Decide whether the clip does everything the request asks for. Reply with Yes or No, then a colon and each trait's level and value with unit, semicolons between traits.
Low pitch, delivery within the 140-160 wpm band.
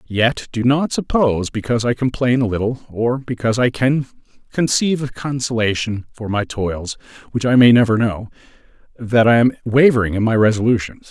No: low, 120 Hz; average, 170 wpm